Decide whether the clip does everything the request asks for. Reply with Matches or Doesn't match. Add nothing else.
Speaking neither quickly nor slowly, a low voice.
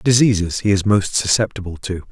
Matches